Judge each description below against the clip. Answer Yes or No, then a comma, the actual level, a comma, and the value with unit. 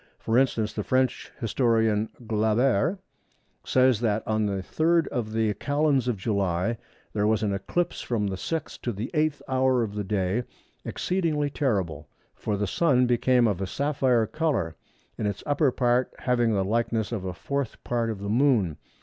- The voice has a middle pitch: No, low, 115 Hz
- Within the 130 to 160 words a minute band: No, average, 170 wpm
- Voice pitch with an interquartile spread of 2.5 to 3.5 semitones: No, average, 4.2 semitones